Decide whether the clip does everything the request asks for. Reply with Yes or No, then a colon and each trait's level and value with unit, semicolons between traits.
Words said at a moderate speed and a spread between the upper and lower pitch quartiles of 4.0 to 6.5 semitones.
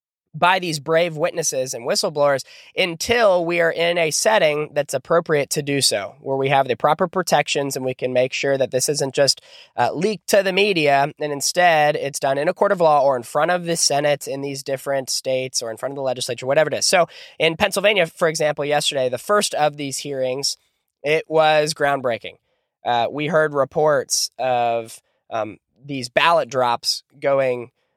No: average, 190 wpm; average, 3.4 semitones